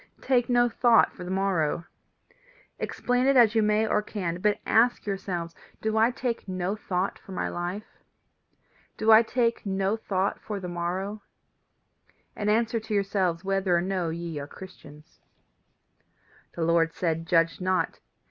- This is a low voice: No, high, 195 Hz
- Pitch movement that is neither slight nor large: Yes, average, 3.9 semitones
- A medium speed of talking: Yes, average, 155 wpm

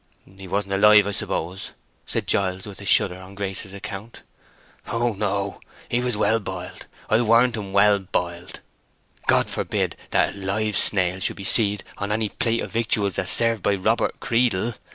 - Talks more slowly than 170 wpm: No, average, 175 wpm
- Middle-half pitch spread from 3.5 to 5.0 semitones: No, narrow, 2.5 semitones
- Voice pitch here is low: Yes, low, 100 Hz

